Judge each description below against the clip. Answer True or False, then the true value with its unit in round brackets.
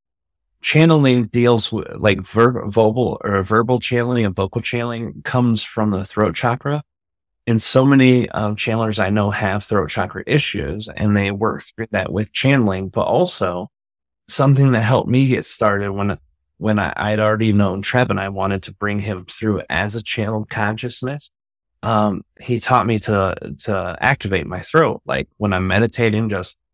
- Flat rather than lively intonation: False (3.2 semitones)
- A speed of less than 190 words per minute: True (165 wpm)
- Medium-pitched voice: False (110 Hz)